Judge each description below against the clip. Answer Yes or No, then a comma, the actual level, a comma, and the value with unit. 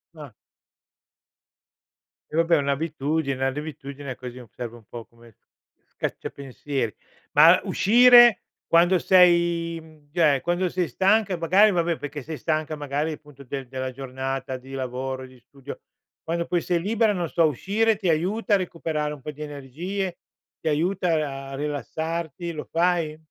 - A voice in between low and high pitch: Yes, medium, 155 Hz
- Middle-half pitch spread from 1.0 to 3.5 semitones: No, average, 4.2 semitones